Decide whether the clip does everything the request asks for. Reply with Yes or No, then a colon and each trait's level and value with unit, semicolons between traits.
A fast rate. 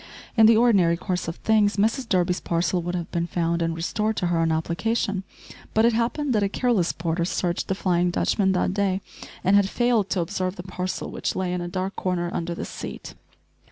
Yes: fast, 210 wpm